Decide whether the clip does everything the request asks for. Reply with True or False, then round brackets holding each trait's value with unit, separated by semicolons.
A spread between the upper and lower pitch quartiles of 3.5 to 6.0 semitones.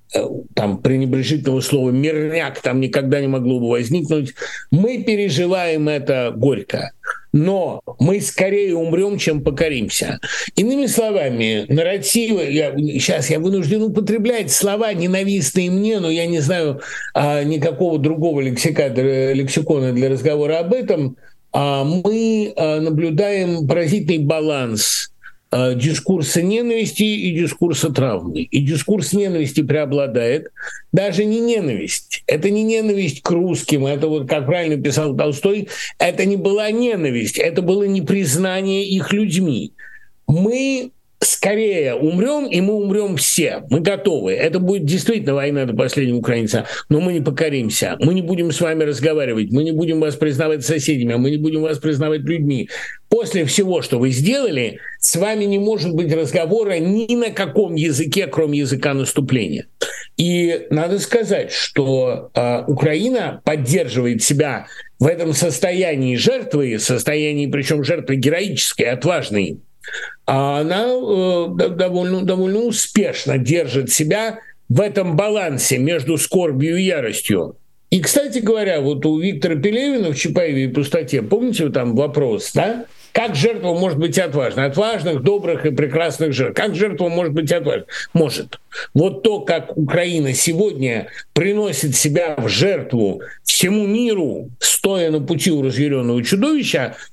True (5.4 semitones)